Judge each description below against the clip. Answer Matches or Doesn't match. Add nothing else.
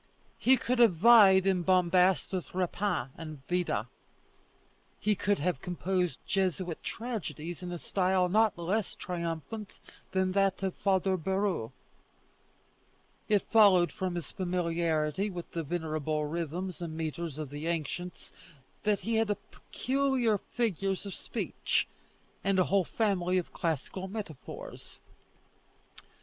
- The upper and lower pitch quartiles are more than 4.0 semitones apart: Doesn't match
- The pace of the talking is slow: Matches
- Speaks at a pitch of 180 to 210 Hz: Matches